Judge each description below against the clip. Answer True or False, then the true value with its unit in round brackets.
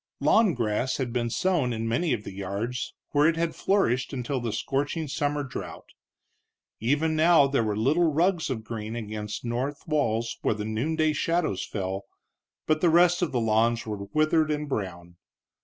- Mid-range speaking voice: False (130 Hz)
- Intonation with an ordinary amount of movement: False (6.0 semitones)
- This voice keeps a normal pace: True (175 wpm)